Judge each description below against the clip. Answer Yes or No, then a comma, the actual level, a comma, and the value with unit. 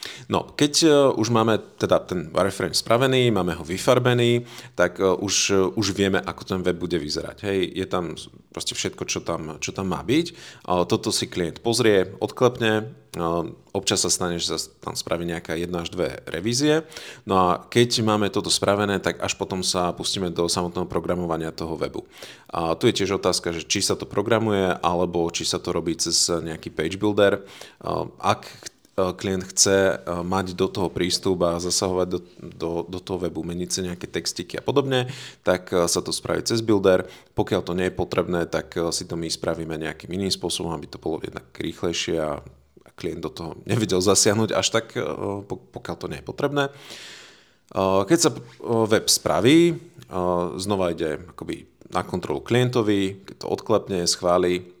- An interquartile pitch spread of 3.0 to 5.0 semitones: Yes, average, 3.9 semitones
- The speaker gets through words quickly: Yes, fast, 170 wpm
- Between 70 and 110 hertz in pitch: Yes, very low, 95 Hz